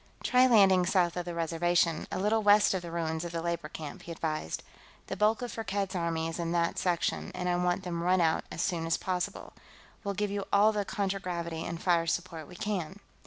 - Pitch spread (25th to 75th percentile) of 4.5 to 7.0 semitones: No, average, 2.8 semitones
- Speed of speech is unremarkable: No, fast, 215 wpm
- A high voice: No, medium, 175 Hz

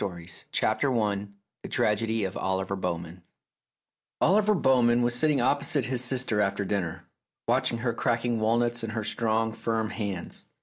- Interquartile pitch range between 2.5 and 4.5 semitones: Yes, average, 3.2 semitones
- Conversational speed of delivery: Yes, average, 145 wpm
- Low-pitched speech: Yes, low, 115 Hz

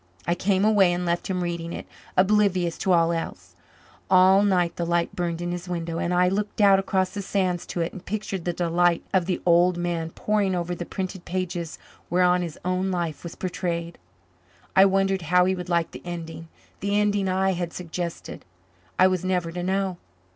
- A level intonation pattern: Yes, narrow, 1.8 semitones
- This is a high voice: No, medium, 180 Hz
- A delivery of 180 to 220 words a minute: Yes, average, 195 wpm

